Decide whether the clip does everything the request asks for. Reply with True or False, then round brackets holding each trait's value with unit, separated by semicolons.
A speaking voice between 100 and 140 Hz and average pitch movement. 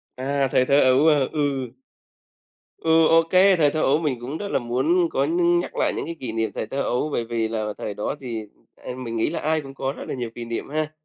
True (135 Hz; 4.8 semitones)